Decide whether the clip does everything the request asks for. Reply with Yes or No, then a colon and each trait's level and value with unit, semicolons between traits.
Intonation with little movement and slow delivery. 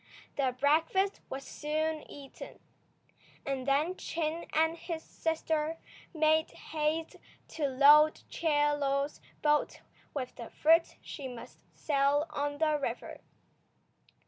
Yes: narrow, 2.2 semitones; slow, 115 wpm